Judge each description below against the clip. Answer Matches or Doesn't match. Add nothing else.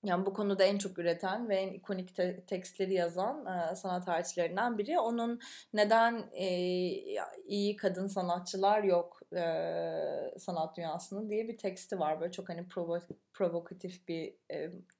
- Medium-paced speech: Matches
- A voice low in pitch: Doesn't match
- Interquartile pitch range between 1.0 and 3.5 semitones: Matches